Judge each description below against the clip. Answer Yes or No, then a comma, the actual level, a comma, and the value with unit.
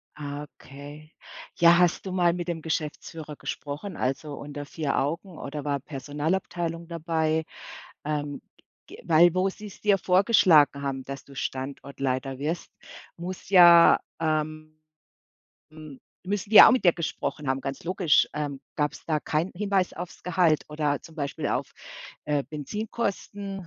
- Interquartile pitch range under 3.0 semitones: No, average, 3.5 semitones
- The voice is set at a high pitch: No, medium, 155 Hz